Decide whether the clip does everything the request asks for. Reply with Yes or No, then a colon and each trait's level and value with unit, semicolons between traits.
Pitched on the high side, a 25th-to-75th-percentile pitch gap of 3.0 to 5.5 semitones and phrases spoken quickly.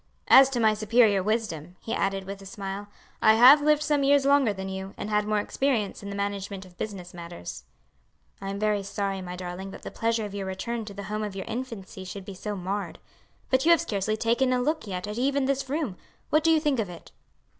Yes: high, 210 Hz; average, 4.4 semitones; fast, 230 wpm